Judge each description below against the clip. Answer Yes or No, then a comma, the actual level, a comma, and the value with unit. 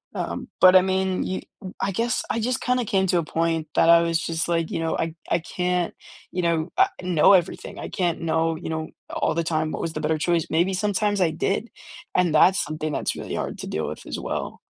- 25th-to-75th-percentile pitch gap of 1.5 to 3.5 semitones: Yes, narrow, 2.6 semitones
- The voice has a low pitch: No, medium, 170 Hz